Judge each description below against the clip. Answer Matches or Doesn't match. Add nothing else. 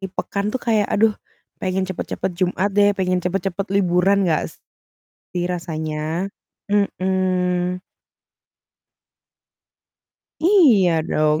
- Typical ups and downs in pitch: Doesn't match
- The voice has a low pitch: Doesn't match